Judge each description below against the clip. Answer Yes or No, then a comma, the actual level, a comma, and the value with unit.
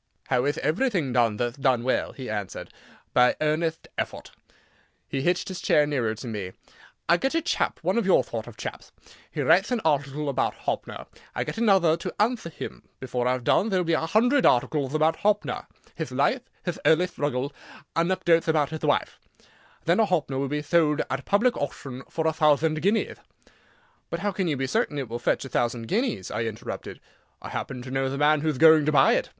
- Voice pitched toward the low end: No, medium, 150 Hz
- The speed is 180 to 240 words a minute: Yes, average, 195 wpm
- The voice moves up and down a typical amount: Yes, average, 5.0 semitones